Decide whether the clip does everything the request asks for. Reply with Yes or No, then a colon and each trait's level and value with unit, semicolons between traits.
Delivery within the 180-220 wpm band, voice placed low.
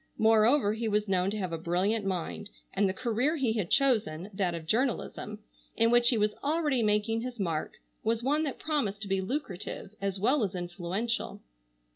No: average, 185 wpm; high, 215 Hz